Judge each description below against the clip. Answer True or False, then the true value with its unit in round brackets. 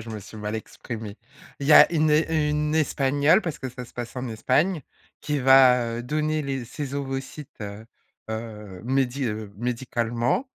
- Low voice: True (130 Hz)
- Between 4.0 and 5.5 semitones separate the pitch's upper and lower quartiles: True (4.4 semitones)